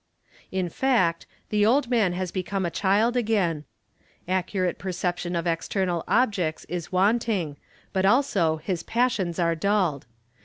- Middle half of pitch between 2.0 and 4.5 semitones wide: Yes, average, 3.7 semitones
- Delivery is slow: Yes, slow, 130 wpm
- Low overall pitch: No, medium, 185 Hz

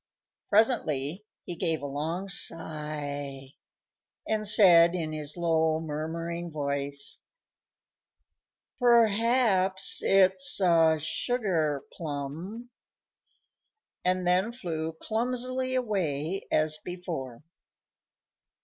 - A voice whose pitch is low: No, medium, 170 Hz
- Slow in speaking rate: Yes, slow, 80 wpm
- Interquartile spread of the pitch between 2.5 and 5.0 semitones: Yes, average, 4.7 semitones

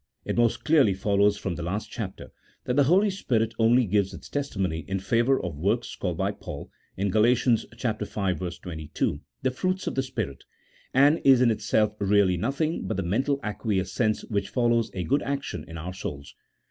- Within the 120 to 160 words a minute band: No, average, 180 wpm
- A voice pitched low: Yes, low, 110 Hz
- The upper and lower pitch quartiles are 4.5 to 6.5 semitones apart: Yes, wide, 5.4 semitones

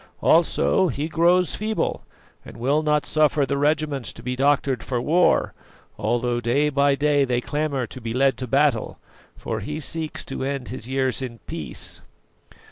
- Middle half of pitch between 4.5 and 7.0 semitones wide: No, average, 3.0 semitones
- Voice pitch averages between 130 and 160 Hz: Yes, medium, 140 Hz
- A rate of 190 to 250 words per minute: No, average, 165 wpm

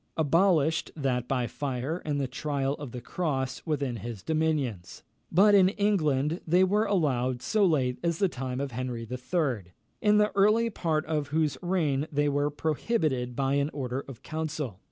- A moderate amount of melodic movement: Yes, average, 4.5 semitones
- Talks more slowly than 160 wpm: No, average, 170 wpm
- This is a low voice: No, medium, 145 Hz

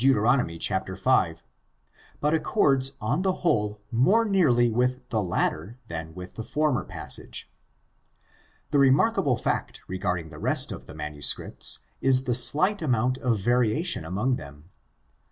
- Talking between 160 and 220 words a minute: No, slow, 135 wpm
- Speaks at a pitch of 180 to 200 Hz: No, low, 120 Hz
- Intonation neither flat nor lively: No, wide, 6.9 semitones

